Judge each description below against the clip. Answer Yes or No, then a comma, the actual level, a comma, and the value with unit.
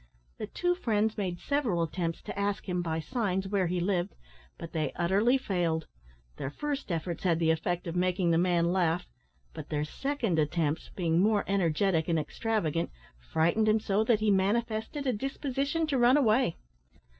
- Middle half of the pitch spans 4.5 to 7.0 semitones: Yes, average, 4.8 semitones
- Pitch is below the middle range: No, high, 190 Hz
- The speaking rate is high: No, average, 170 wpm